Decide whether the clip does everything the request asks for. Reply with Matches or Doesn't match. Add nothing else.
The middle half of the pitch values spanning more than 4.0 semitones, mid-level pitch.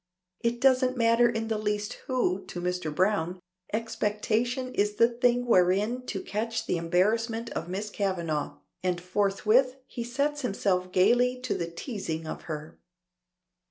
Doesn't match